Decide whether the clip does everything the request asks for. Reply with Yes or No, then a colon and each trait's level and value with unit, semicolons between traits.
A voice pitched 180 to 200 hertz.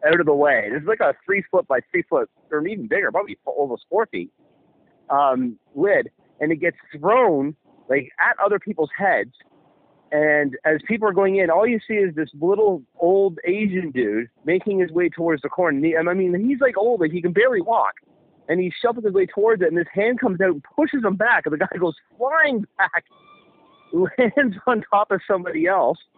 Yes: medium, 185 Hz